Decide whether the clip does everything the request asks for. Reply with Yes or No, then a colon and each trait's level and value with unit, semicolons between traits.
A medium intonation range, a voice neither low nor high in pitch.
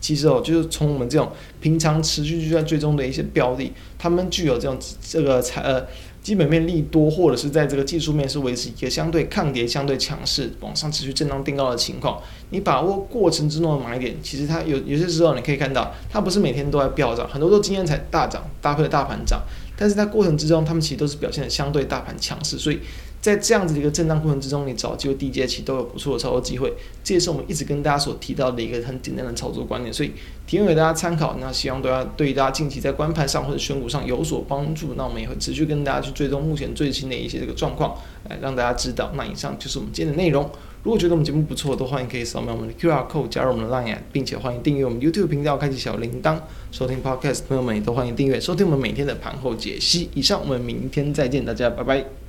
Yes: average, 3.5 semitones; medium, 145 Hz